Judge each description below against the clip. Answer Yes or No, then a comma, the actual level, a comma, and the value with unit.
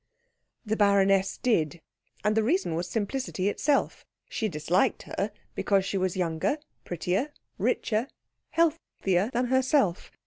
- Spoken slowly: Yes, slow, 125 wpm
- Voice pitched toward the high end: Yes, high, 205 Hz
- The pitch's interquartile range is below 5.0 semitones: No, wide, 5.5 semitones